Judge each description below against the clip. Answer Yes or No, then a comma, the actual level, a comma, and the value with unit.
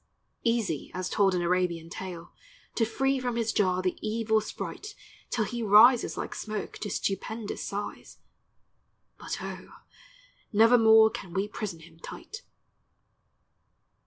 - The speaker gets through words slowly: Yes, slow, 130 wpm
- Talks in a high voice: Yes, high, 215 Hz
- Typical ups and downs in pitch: Yes, average, 3.8 semitones